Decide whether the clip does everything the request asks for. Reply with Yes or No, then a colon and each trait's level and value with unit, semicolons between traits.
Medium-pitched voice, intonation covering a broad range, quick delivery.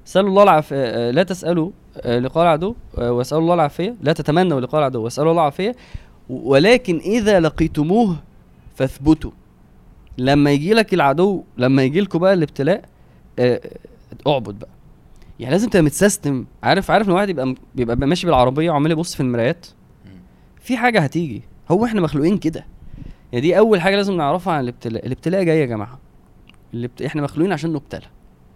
Yes: medium, 155 Hz; wide, 6.5 semitones; fast, 155 wpm